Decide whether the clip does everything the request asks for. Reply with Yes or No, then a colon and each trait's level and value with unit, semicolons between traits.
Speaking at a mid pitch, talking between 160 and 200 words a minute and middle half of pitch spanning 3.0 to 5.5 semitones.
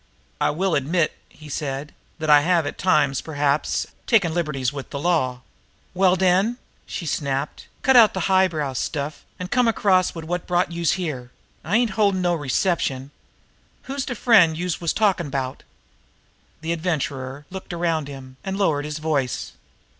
Yes: medium, 165 Hz; average, 165 wpm; average, 4.5 semitones